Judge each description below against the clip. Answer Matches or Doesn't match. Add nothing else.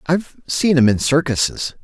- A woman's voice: Doesn't match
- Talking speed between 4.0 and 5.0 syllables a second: Matches